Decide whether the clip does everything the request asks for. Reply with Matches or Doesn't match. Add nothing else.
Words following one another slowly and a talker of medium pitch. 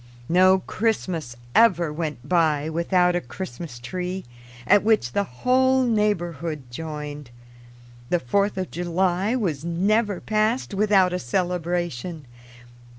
Matches